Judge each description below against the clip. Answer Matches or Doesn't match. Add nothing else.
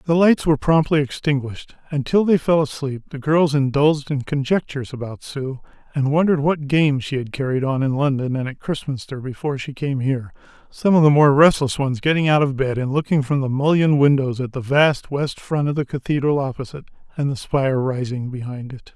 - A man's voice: Matches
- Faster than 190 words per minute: Matches